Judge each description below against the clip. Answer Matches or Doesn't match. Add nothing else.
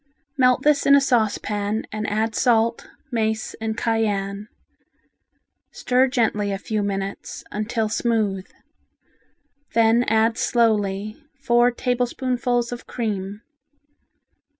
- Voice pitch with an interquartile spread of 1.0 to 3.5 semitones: Matches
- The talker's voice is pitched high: Matches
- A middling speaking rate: Doesn't match